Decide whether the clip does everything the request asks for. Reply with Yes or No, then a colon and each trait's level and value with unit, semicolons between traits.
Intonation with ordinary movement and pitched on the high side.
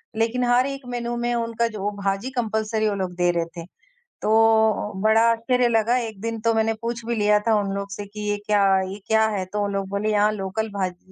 No: narrow, 2.3 semitones; high, 220 Hz